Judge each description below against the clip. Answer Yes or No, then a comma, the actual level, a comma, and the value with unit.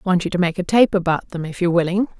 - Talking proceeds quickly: Yes, fast, 300 wpm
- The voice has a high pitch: No, medium, 180 Hz